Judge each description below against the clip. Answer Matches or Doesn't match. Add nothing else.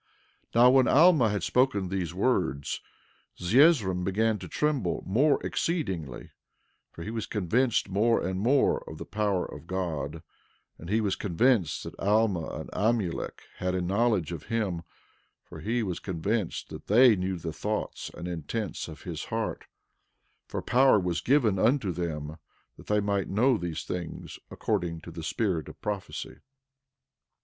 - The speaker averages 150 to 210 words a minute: Matches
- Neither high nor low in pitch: Doesn't match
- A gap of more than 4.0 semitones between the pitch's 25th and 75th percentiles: Matches